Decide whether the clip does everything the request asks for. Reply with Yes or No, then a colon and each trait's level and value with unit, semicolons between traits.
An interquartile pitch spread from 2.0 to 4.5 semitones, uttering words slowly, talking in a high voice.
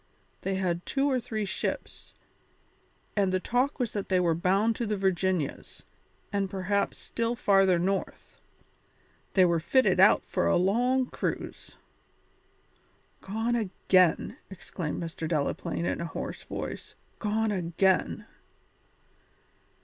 Yes: average, 3.7 semitones; slow, 125 wpm; high, 195 Hz